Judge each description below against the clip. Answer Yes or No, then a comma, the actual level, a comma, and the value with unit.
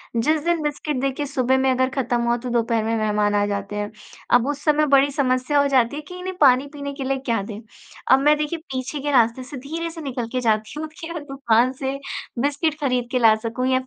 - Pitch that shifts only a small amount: No, average, 3.6 semitones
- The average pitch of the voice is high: Yes, very high, 265 Hz